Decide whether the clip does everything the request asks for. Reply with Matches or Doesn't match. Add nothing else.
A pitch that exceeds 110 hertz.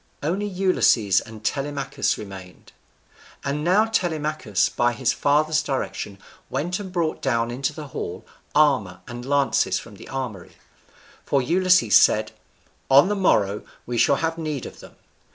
Matches